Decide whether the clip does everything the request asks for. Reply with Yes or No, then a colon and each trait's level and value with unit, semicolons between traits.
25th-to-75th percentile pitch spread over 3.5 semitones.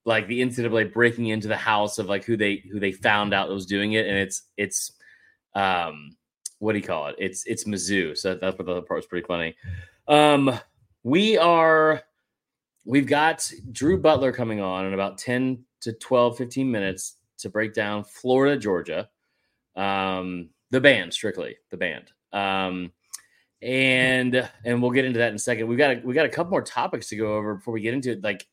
Yes: average, 4.5 semitones